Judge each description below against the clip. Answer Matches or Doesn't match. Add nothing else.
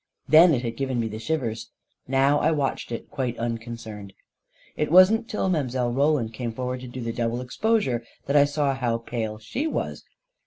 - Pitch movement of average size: Matches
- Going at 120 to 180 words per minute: Doesn't match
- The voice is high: Doesn't match